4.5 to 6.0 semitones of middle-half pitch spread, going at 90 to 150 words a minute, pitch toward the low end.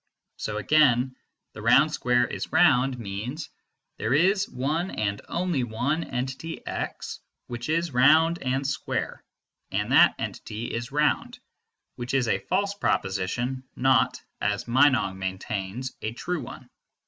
Yes: average, 4.9 semitones; slow, 135 wpm; low, 130 Hz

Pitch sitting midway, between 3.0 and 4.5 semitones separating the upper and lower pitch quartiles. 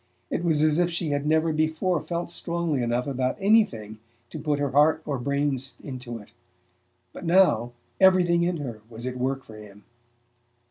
No: medium, 145 Hz; average, 5.1 semitones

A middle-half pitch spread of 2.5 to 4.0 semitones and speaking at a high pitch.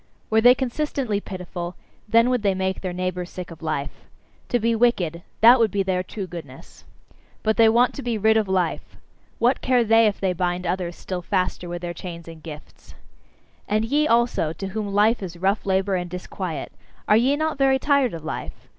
No: average, 4.7 semitones; high, 195 Hz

